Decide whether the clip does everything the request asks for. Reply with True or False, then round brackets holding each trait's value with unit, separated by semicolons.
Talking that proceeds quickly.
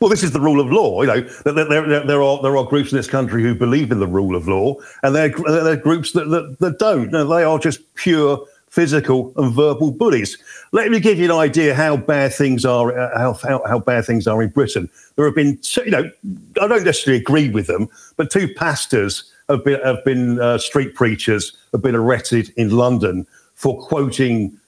True (225 wpm)